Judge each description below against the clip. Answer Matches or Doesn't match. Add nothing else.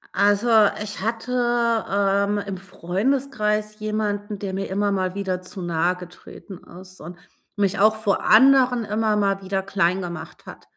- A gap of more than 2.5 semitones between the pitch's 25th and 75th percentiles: Doesn't match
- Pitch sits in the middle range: Doesn't match